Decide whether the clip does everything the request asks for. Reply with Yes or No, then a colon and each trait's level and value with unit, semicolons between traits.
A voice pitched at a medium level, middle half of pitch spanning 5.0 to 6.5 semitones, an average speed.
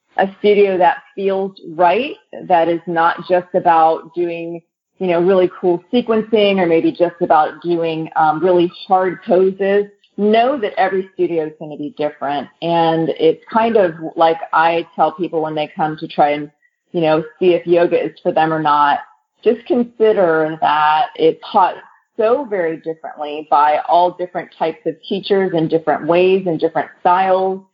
No: medium, 175 Hz; average, 2.9 semitones; average, 170 wpm